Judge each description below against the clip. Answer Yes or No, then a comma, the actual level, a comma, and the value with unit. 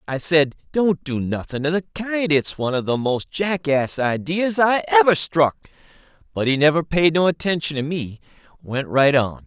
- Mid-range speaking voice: Yes, medium, 150 Hz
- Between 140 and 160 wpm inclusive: No, average, 185 wpm